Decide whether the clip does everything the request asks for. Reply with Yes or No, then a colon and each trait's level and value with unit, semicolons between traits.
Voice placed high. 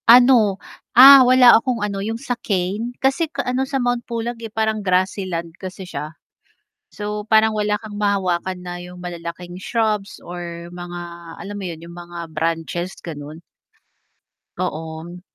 Yes: high, 195 Hz